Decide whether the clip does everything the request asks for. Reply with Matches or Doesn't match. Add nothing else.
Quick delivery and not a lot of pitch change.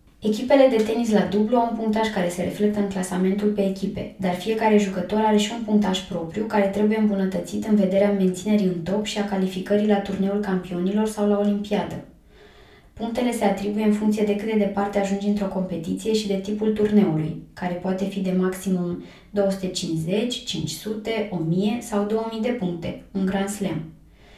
Matches